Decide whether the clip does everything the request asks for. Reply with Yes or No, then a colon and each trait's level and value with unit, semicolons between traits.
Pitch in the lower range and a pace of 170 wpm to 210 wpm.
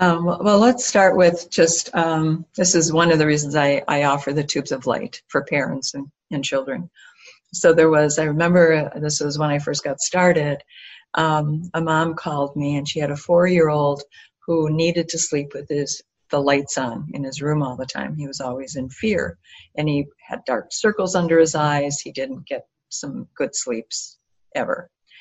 No: medium, 150 Hz; average, 200 wpm